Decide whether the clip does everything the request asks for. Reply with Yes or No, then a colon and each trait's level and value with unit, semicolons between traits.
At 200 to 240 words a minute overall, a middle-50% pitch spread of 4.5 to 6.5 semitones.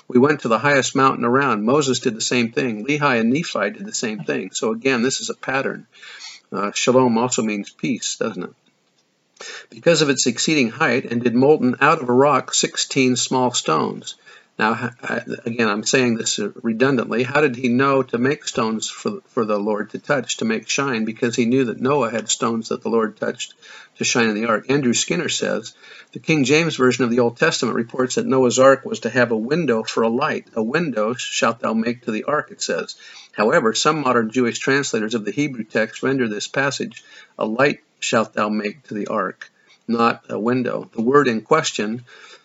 No: fast, 205 wpm; average, 2.9 semitones